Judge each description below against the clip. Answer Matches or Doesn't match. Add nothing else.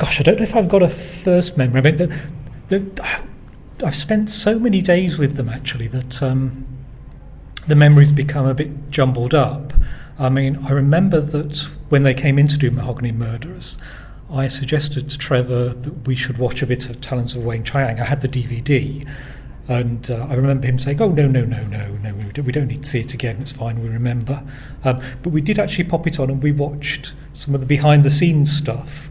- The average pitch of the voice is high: Doesn't match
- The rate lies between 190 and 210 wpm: Matches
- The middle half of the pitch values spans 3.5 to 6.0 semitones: Doesn't match